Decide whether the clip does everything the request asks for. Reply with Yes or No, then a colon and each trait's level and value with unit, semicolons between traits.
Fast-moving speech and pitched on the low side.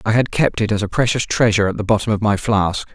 Yes: fast, 285 wpm; low, 110 Hz